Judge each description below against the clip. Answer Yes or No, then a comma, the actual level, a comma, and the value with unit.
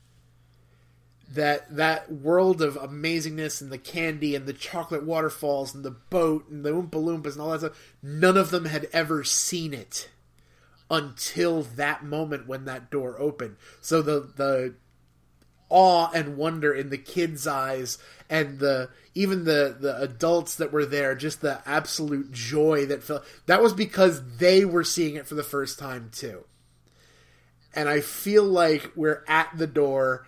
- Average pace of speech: Yes, average, 165 wpm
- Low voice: No, medium, 150 Hz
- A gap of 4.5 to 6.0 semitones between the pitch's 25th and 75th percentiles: No, average, 3.4 semitones